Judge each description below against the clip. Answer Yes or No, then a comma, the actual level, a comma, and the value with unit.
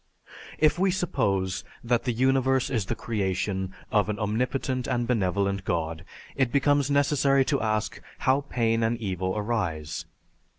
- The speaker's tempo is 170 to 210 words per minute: No, average, 140 wpm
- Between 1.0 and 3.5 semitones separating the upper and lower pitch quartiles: No, average, 5.2 semitones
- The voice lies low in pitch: Yes, low, 115 Hz